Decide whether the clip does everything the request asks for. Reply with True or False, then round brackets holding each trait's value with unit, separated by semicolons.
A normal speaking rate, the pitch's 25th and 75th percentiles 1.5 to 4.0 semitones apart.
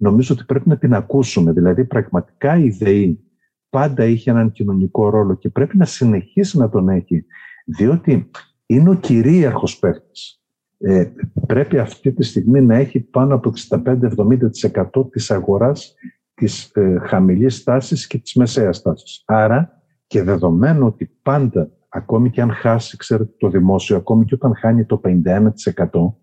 False (150 wpm; 5.1 semitones)